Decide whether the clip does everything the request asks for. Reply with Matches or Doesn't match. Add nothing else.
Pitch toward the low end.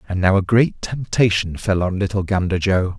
Matches